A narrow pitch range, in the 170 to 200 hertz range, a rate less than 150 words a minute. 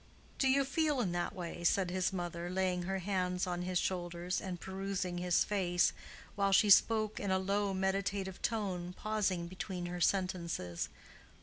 No: narrow, 2.0 semitones; medium, 185 Hz; average, 165 wpm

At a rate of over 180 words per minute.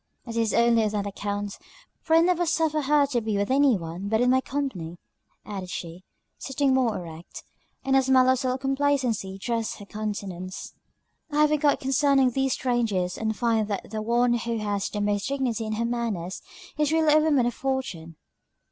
Yes: average, 190 wpm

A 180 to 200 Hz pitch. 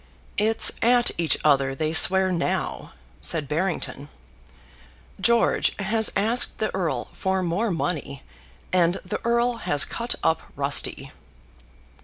Yes: medium, 185 Hz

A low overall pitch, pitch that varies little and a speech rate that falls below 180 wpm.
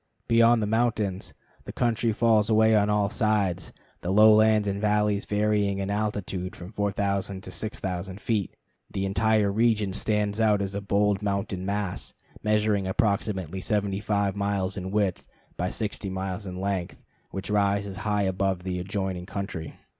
Yes: low, 100 Hz; narrow, 1.8 semitones; average, 150 wpm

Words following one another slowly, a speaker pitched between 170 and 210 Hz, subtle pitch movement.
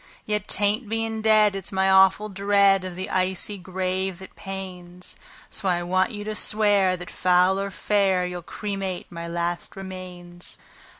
No: average, 160 wpm; high, 190 Hz; narrow, 2.0 semitones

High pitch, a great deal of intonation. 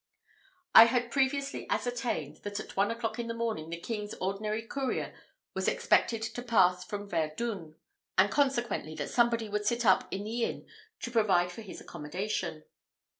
No: high, 220 Hz; average, 3.9 semitones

